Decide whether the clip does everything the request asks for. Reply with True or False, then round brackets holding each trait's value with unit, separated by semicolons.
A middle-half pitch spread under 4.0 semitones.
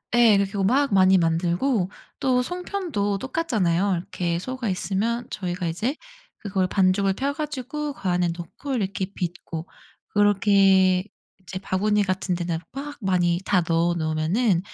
False (5.2 semitones)